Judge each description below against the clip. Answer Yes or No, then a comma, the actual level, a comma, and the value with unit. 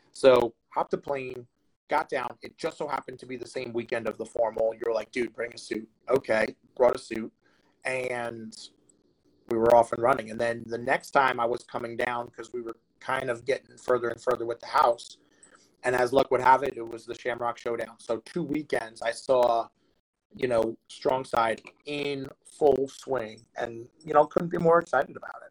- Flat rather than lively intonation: Yes, narrow, 2.0 semitones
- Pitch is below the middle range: Yes, low, 120 Hz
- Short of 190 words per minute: No, fast, 205 wpm